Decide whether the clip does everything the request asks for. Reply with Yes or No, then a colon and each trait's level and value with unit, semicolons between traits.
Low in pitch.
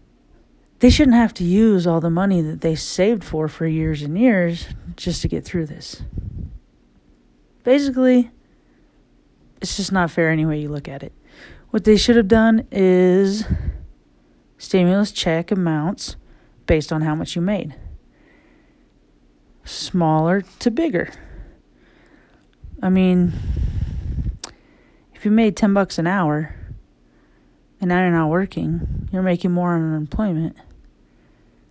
No: medium, 165 Hz